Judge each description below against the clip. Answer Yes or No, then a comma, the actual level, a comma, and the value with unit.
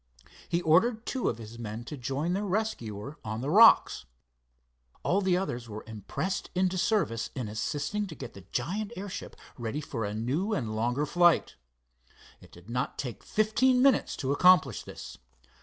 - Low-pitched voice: No, medium, 145 Hz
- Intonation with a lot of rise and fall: Yes, wide, 8.8 semitones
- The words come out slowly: No, average, 165 wpm